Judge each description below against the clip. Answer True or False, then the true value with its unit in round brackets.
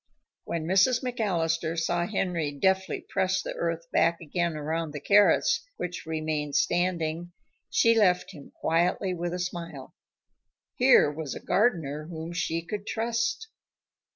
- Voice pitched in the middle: True (170 Hz)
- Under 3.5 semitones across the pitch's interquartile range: True (2.9 semitones)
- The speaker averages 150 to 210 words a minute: False (135 wpm)